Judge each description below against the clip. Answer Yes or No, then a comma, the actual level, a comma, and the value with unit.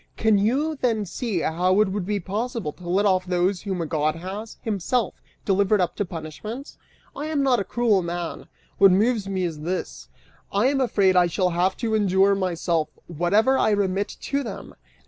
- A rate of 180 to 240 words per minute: Yes, average, 185 wpm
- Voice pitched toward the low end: No, high, 195 Hz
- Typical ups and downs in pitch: Yes, average, 3.6 semitones